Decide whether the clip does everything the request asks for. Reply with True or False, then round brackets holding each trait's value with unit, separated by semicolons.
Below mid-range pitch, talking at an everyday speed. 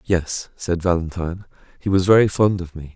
True (90 Hz; 185 wpm)